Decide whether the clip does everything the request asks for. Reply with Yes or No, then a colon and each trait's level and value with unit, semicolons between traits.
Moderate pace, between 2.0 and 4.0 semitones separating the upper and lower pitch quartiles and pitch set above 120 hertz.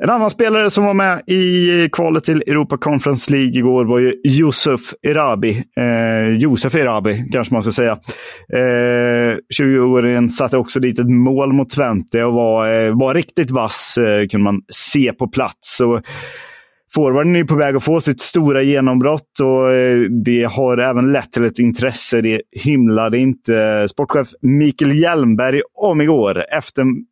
Yes: average, 155 wpm; average, 3.5 semitones; low, 130 Hz